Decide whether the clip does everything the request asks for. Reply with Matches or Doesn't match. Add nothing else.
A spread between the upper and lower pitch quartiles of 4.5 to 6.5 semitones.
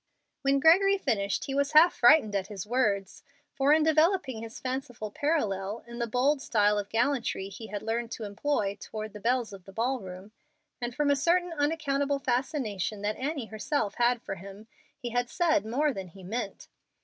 Matches